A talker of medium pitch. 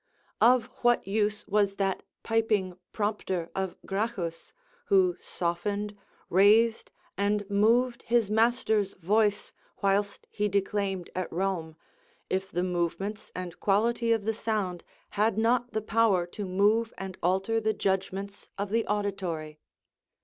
No: high, 200 Hz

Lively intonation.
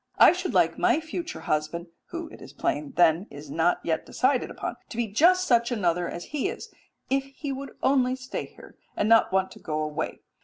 Yes: wide, 9.0 semitones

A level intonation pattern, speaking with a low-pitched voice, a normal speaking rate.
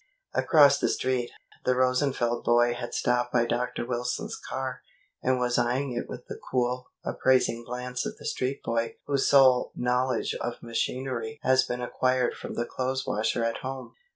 Yes: narrow, 1.3 semitones; low, 125 Hz; average, 165 wpm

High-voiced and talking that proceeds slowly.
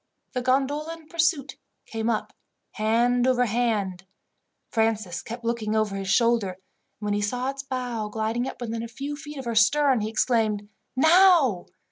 No: high, 235 Hz; average, 165 wpm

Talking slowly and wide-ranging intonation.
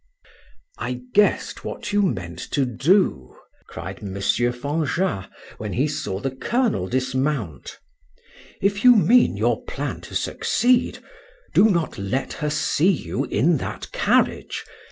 Yes: slow, 130 wpm; wide, 8.3 semitones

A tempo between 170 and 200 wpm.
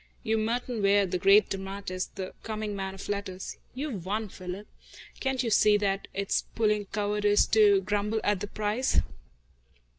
No: average, 155 wpm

